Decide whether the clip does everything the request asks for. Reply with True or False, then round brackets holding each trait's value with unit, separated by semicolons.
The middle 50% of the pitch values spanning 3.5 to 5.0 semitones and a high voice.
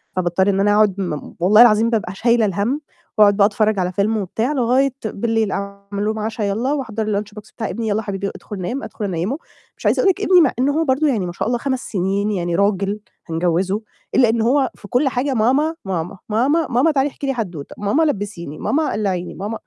True (4.1 semitones; 215 Hz)